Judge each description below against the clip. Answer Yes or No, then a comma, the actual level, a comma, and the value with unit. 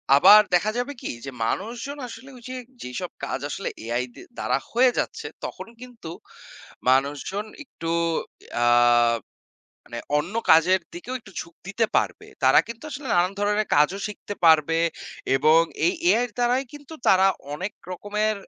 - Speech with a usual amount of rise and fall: No, wide, 6.9 semitones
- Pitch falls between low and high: No, high, 205 Hz